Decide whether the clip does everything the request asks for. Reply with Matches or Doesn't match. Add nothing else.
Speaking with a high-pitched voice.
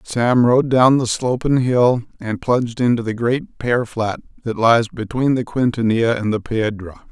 Doesn't match